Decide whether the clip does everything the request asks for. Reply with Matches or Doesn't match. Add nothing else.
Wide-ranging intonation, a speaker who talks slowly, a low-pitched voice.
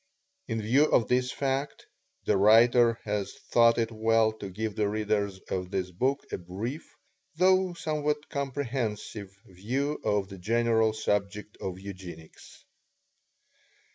Doesn't match